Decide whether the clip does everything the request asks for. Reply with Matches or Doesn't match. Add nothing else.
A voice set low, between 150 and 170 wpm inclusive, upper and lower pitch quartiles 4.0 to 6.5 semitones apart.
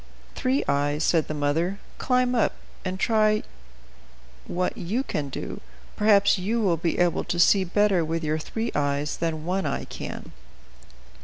Doesn't match